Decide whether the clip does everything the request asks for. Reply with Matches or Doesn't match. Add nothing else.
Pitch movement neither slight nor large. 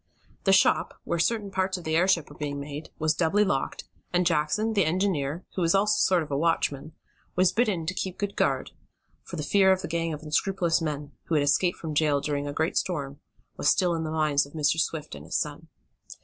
Matches